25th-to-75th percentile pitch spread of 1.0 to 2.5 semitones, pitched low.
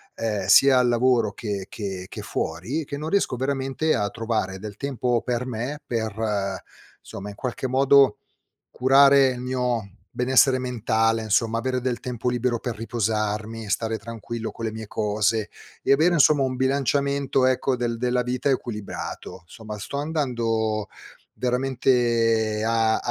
No: average, 2.9 semitones; low, 120 Hz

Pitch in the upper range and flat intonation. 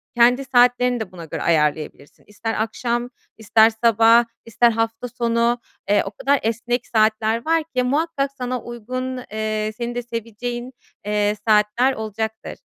Yes: high, 230 Hz; narrow, 2.3 semitones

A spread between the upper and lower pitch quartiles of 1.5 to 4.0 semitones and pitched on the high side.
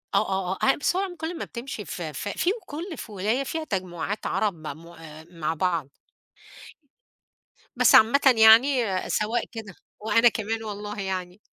No: average, 5.0 semitones; high, 210 Hz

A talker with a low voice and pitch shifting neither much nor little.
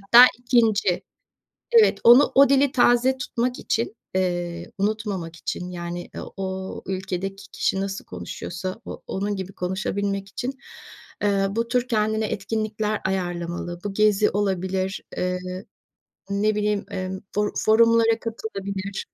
No: high, 200 Hz; average, 3.1 semitones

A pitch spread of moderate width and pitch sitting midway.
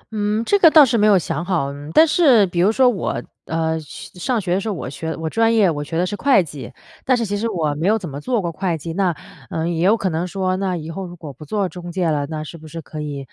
Yes: average, 4.5 semitones; medium, 180 Hz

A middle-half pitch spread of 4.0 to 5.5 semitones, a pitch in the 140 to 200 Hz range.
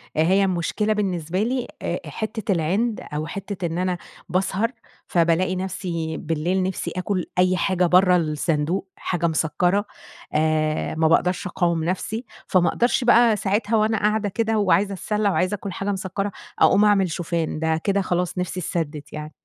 No: average, 3.4 semitones; medium, 185 Hz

